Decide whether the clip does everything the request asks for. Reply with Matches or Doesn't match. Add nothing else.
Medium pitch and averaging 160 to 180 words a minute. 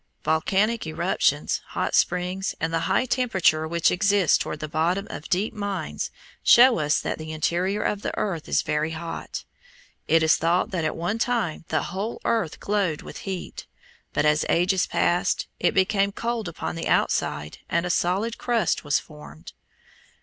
Matches